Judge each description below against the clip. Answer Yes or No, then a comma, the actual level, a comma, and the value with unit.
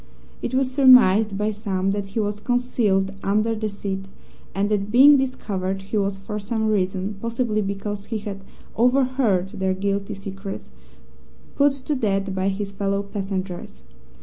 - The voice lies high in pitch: Yes, high, 200 Hz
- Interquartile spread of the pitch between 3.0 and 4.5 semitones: No, narrow, 2.5 semitones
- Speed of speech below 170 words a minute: Yes, average, 150 wpm